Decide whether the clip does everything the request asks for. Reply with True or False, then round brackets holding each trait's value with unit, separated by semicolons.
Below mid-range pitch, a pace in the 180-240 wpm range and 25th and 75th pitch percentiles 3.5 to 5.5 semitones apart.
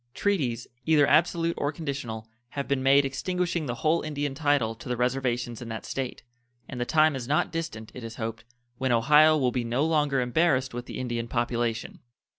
True (130 Hz; 190 wpm; 4.2 semitones)